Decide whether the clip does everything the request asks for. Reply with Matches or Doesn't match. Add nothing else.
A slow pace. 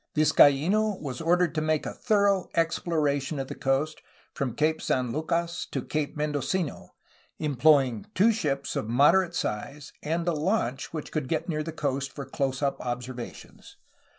Doesn't match